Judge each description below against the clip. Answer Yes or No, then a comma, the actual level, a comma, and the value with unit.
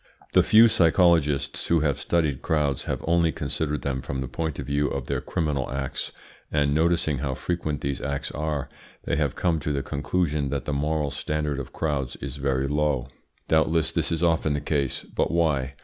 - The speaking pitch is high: No, very low, 75 Hz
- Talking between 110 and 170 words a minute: No, average, 190 wpm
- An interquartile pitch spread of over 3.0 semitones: No, narrow, 2.4 semitones